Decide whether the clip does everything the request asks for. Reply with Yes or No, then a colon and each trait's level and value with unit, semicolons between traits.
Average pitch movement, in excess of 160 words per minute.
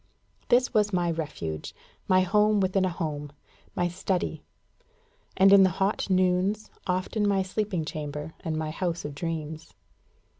No: average, 3.5 semitones; average, 145 wpm